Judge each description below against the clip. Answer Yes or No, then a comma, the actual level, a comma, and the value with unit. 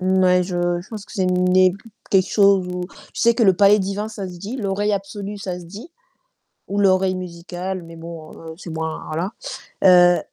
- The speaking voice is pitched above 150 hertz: Yes, medium, 185 Hz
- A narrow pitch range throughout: Yes, narrow, 2.1 semitones